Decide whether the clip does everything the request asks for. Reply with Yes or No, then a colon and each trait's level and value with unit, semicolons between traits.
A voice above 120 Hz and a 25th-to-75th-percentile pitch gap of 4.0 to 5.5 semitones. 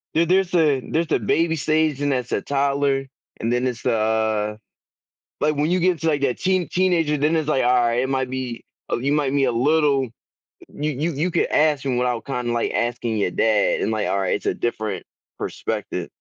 Yes: low, 135 Hz; average, 4.3 semitones